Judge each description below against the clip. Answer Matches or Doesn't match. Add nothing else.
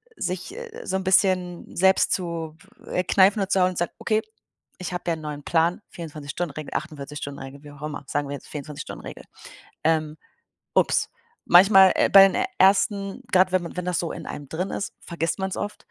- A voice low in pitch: Doesn't match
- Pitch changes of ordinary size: Matches